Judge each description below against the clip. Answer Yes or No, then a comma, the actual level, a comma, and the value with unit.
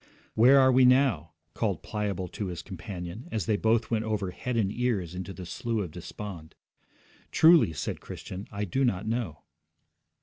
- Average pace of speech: Yes, average, 170 wpm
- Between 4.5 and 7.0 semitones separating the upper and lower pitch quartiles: Yes, average, 4.9 semitones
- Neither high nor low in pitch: No, low, 105 Hz